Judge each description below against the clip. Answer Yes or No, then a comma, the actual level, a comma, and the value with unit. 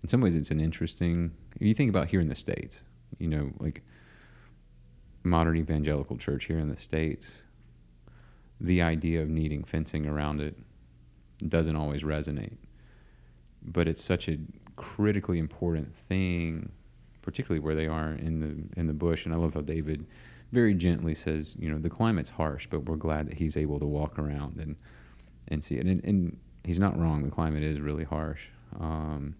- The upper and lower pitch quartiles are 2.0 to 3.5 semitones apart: Yes, narrow, 2.6 semitones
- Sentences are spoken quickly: No, average, 180 wpm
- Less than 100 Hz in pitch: Yes, very low, 75 Hz